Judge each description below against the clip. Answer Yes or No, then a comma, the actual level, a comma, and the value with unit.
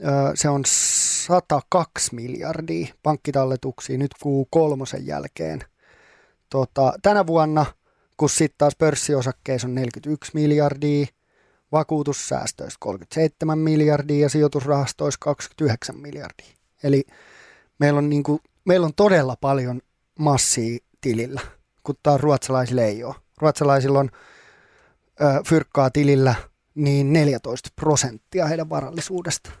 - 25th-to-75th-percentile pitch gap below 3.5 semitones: Yes, average, 2.7 semitones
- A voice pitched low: No, medium, 145 Hz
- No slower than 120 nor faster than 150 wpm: No, average, 105 wpm